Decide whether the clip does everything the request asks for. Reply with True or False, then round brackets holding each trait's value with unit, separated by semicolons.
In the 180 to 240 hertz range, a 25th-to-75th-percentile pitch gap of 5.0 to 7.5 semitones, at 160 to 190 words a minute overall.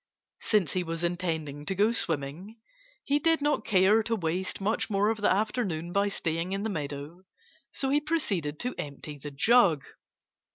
True (190 Hz; 5.6 semitones; 170 wpm)